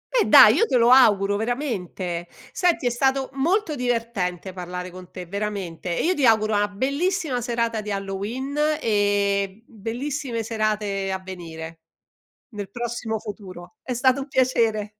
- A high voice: Yes, high, 215 Hz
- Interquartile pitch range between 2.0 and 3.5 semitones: No, average, 4.5 semitones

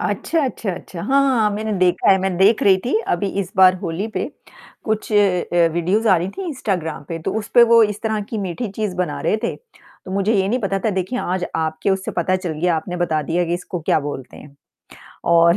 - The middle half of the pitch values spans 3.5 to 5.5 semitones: Yes, average, 3.8 semitones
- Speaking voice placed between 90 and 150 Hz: No, high, 190 Hz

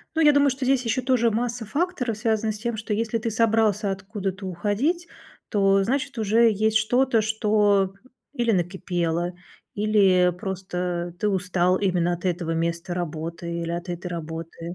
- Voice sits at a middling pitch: No, high, 205 Hz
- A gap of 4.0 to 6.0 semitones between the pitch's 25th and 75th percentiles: Yes, average, 4.3 semitones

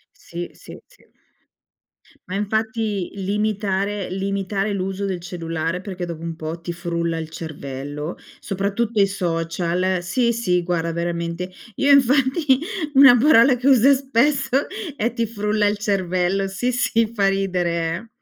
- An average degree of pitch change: Yes, average, 4.6 semitones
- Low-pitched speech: No, high, 195 Hz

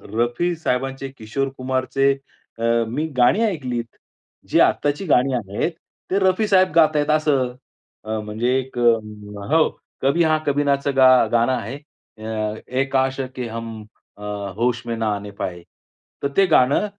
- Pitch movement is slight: No, average, 4.1 semitones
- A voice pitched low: Yes, low, 130 Hz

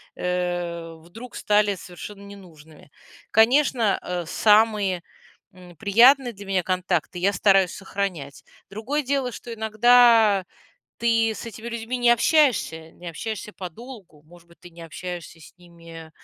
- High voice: Yes, high, 195 Hz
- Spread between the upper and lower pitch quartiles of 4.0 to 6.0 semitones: Yes, average, 4.6 semitones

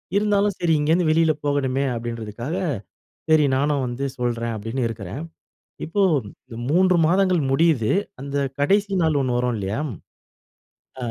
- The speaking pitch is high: No, medium, 145 Hz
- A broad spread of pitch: Yes, wide, 5.9 semitones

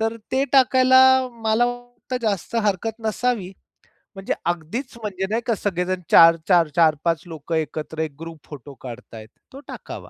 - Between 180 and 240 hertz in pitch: Yes, medium, 185 Hz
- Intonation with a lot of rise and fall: Yes, wide, 6.4 semitones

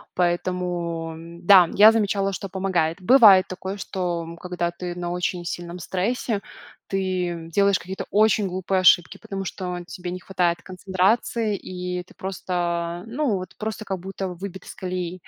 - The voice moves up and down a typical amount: No, narrow, 1.8 semitones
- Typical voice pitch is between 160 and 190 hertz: Yes, medium, 185 Hz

